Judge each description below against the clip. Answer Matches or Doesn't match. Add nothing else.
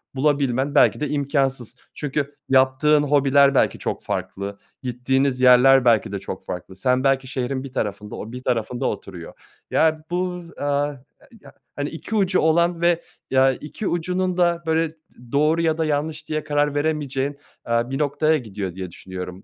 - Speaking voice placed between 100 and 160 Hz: Matches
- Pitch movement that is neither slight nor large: Matches